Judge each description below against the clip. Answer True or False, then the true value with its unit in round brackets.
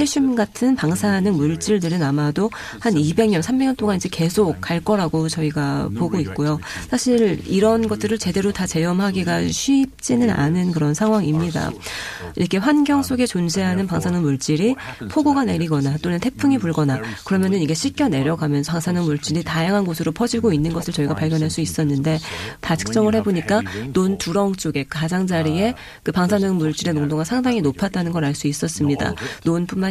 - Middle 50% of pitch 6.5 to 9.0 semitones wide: False (5.2 semitones)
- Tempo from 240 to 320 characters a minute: False (370 characters per minute)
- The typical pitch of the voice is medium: True (180 Hz)